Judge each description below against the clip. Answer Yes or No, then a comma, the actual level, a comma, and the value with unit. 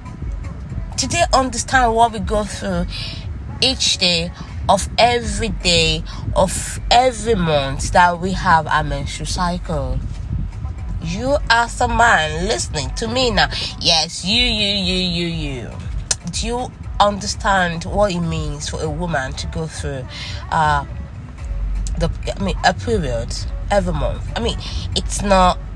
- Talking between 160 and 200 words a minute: No, slow, 135 wpm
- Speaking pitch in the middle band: Yes, medium, 160 Hz